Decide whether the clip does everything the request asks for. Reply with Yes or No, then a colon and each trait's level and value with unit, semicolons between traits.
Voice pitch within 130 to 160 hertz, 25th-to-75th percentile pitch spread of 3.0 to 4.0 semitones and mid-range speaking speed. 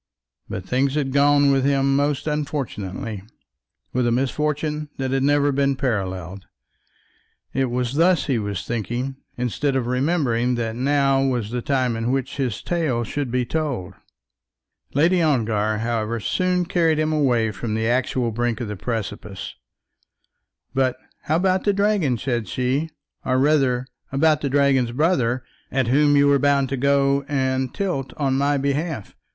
Yes: low, 135 Hz; average, 3.3 semitones; average, 155 wpm